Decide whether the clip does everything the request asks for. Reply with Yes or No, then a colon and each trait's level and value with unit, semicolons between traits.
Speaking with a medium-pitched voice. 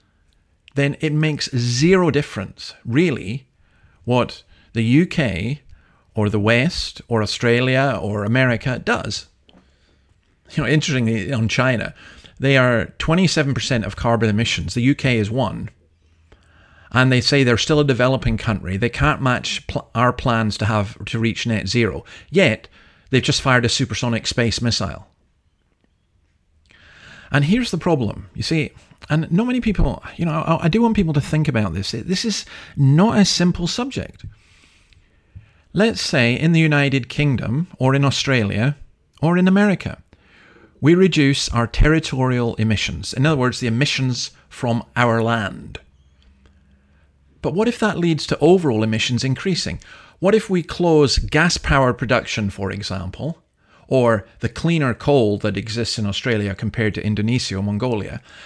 No: low, 120 Hz